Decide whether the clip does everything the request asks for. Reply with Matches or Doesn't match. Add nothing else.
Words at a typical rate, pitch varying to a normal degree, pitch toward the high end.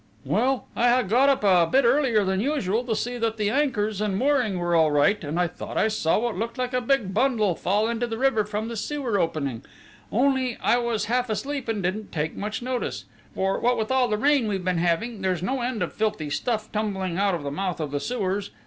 Doesn't match